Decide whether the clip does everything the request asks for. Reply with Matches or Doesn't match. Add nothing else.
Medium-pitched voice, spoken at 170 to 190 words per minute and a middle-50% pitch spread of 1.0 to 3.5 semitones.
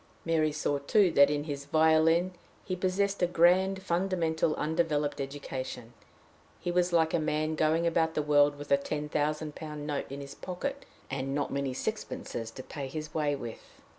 Matches